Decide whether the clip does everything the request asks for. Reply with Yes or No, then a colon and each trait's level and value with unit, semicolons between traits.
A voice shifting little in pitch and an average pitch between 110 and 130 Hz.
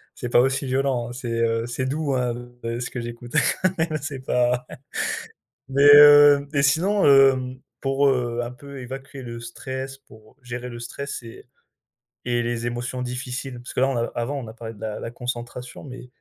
Yes: narrow, 2.3 semitones; low, 125 Hz